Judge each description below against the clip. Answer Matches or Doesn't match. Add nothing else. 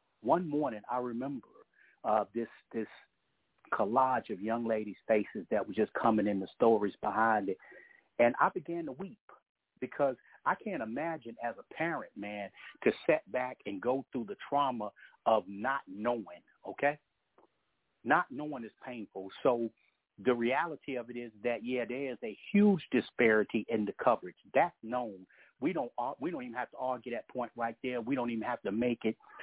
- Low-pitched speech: Matches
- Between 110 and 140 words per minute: Doesn't match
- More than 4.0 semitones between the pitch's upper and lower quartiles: Doesn't match